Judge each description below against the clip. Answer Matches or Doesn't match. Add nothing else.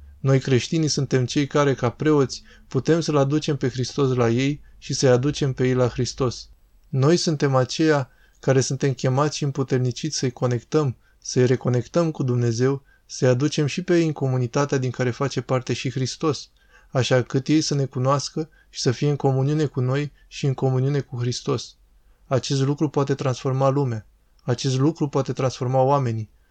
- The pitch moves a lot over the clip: Doesn't match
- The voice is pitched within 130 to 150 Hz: Matches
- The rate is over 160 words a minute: Matches